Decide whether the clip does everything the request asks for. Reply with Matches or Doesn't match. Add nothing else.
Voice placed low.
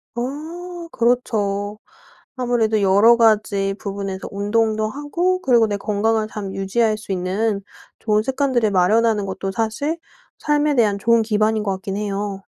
Doesn't match